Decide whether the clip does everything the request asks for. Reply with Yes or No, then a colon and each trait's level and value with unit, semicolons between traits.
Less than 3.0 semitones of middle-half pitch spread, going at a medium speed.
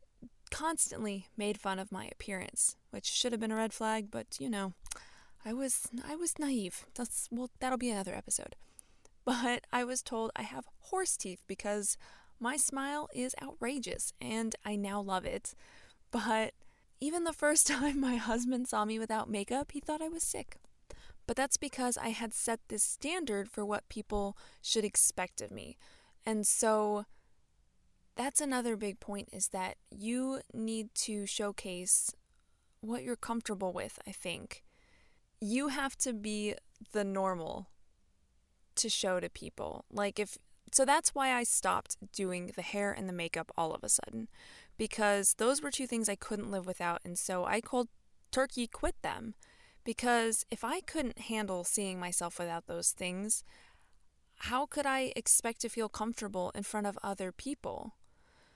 No: average, 3.9 semitones; average, 165 wpm